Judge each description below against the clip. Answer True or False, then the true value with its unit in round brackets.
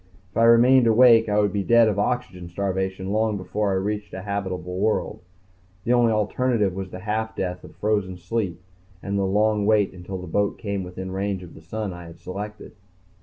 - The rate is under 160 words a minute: False (200 wpm)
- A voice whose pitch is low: True (100 Hz)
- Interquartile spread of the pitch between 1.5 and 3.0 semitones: True (2.6 semitones)